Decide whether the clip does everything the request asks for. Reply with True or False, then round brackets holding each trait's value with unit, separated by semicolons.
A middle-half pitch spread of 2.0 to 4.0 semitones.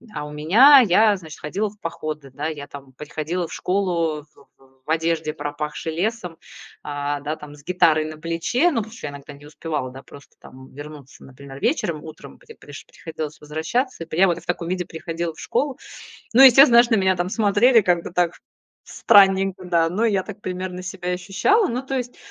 False (5.0 semitones)